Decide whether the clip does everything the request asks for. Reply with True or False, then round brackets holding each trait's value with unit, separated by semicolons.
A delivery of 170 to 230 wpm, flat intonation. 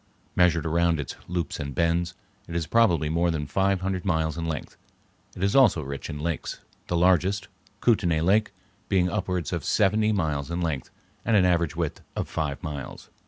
False (180 wpm; 3.1 semitones)